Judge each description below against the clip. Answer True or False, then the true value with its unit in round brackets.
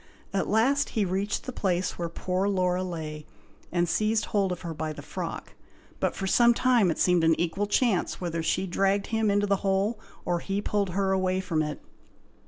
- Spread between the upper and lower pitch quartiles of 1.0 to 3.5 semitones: True (2.9 semitones)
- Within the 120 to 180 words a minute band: False (195 wpm)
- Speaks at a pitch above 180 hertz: True (190 Hz)